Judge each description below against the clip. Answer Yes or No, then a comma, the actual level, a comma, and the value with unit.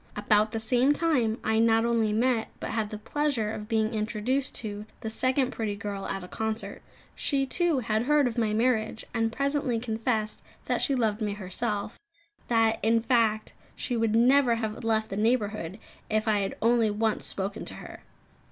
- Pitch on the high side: Yes, high, 225 Hz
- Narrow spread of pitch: Yes, narrow, 2.3 semitones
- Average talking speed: Yes, average, 180 wpm